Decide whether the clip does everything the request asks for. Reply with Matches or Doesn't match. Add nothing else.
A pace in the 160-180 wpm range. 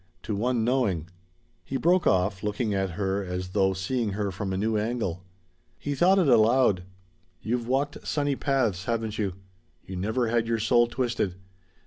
Matches